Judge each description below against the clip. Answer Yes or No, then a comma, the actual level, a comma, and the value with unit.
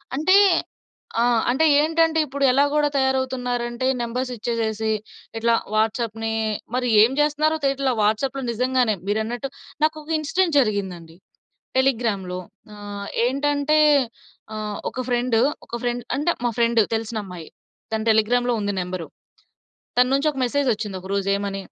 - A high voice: Yes, high, 240 Hz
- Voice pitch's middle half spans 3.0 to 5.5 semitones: Yes, average, 4.1 semitones